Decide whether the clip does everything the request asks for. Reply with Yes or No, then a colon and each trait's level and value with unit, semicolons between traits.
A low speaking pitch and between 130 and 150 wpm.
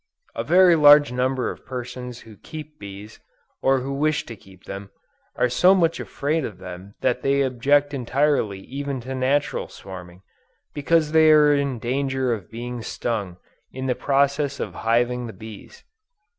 No: low, 130 Hz; average, 160 wpm